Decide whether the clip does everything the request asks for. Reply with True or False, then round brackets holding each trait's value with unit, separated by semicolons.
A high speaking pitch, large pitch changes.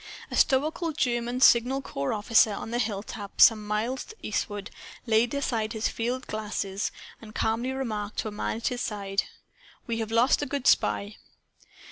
False (225 Hz; 2.9 semitones)